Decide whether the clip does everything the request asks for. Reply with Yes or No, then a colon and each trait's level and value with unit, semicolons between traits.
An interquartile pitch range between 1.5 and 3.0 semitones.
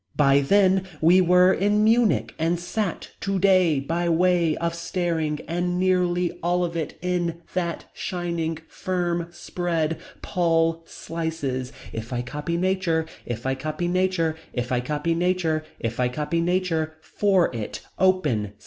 Yes: narrow, 2.6 semitones